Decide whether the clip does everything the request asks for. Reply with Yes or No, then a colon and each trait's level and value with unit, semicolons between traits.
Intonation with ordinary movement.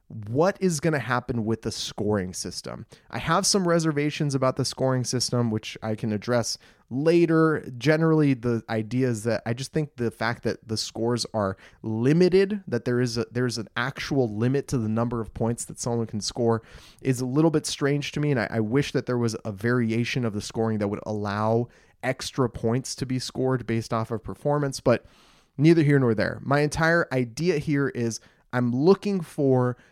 Yes: average, 4.1 semitones